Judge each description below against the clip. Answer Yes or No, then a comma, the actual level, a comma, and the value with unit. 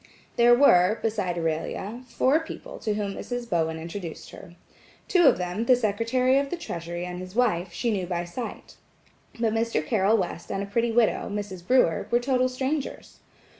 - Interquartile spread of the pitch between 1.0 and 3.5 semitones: No, wide, 5.5 semitones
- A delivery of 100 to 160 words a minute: No, average, 170 wpm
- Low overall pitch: No, high, 210 Hz